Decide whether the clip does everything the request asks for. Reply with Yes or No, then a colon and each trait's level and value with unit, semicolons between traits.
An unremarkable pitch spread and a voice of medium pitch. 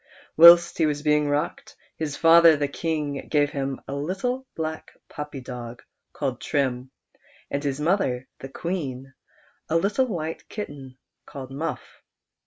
Yes: average, 3.4 semitones; medium, 150 Hz